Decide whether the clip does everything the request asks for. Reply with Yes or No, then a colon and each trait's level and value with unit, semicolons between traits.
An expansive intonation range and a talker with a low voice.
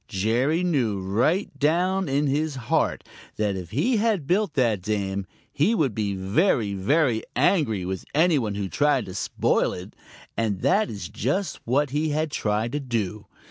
Yes: wide, 7.2 semitones; low, 125 Hz